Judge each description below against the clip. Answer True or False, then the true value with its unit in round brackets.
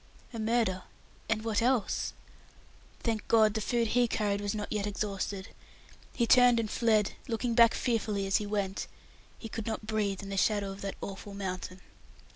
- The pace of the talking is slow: False (175 wpm)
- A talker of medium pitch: False (215 Hz)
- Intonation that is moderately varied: False (2.3 semitones)